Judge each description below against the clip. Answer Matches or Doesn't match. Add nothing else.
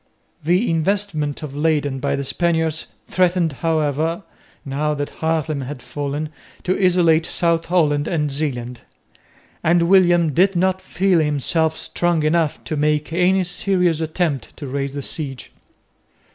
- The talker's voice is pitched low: Doesn't match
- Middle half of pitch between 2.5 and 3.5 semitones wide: Matches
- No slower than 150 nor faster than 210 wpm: Doesn't match